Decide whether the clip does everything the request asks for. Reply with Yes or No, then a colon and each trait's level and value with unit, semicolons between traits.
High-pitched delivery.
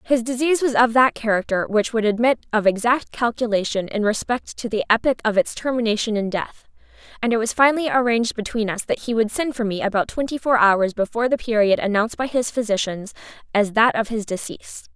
Yes: high, 225 Hz